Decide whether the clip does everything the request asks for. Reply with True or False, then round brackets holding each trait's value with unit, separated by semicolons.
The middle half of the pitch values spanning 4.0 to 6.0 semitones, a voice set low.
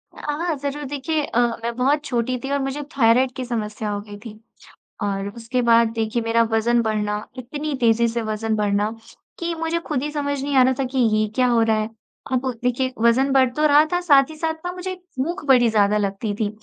False (4.3 semitones; 250 Hz)